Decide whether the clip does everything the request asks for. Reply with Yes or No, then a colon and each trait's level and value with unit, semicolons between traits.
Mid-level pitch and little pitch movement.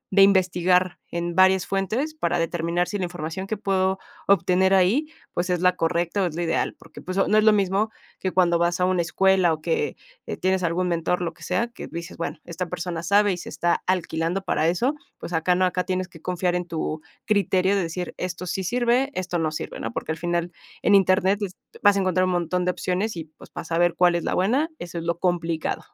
Yes: medium, 180 Hz; narrow, 1.9 semitones